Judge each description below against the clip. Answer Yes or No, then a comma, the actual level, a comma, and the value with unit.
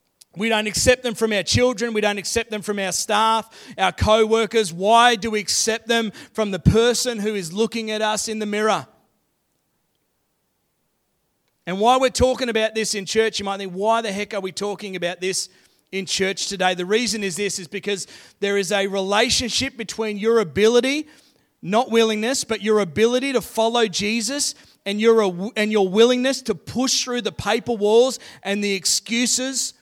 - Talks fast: No, average, 180 wpm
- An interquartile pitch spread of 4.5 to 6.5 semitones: No, narrow, 2.6 semitones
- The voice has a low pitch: No, high, 220 Hz